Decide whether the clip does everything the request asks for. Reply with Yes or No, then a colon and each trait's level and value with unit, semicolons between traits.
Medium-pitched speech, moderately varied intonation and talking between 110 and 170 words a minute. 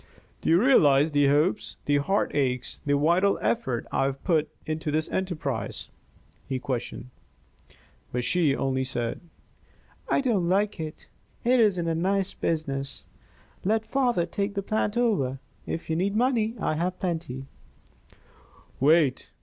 No: medium, 165 Hz; wide, 6.3 semitones; average, 140 wpm